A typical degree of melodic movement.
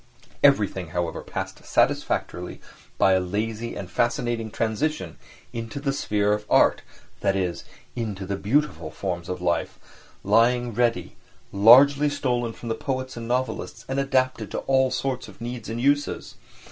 Yes: average, 4.9 semitones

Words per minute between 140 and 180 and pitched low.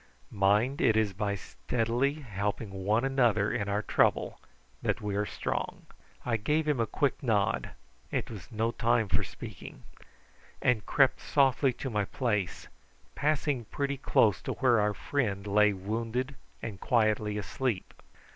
Yes: average, 145 wpm; low, 110 Hz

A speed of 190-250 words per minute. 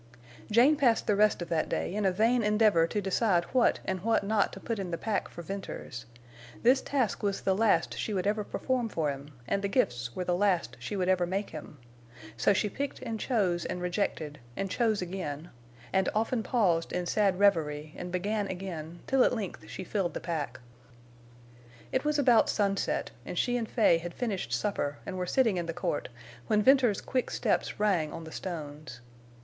Yes: average, 200 wpm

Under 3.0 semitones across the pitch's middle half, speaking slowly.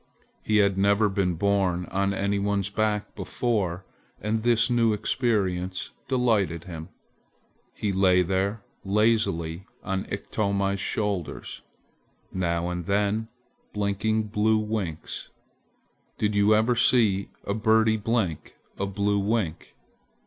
Yes: narrow, 2.4 semitones; slow, 115 wpm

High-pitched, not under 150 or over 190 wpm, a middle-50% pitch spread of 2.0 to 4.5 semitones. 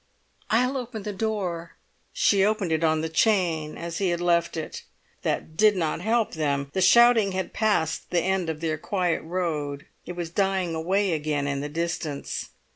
No: medium, 175 Hz; average, 180 wpm; average, 3.9 semitones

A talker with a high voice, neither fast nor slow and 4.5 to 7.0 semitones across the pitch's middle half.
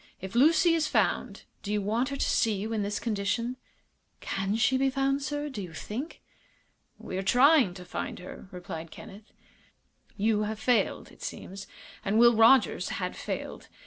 Yes: high, 220 Hz; average, 175 wpm; average, 5.1 semitones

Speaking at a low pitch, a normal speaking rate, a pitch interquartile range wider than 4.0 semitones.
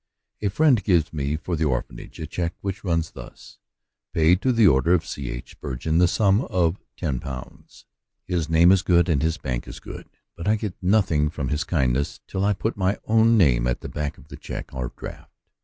No: very low, 85 Hz; fast, 210 wpm; average, 4.9 semitones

